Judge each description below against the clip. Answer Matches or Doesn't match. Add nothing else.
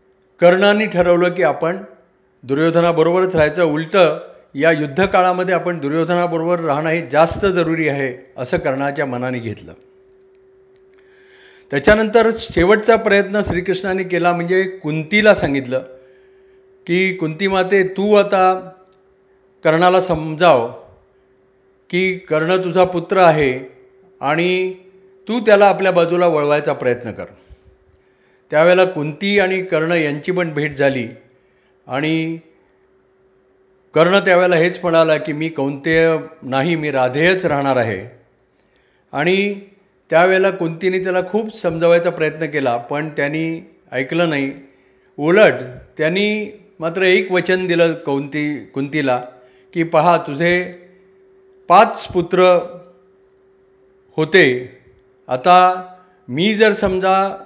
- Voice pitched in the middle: Matches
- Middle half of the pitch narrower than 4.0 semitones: Doesn't match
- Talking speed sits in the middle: Matches